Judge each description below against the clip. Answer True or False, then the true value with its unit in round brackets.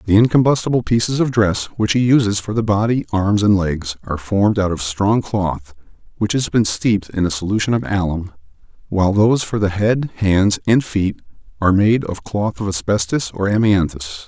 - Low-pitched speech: True (100 Hz)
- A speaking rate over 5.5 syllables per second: False (5.3 syllables/s)